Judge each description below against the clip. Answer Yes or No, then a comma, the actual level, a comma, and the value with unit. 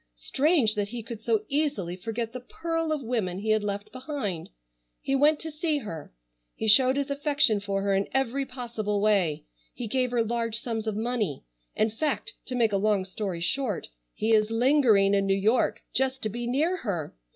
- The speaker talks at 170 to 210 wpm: Yes, average, 195 wpm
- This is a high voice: Yes, high, 230 Hz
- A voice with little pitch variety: No, average, 4.7 semitones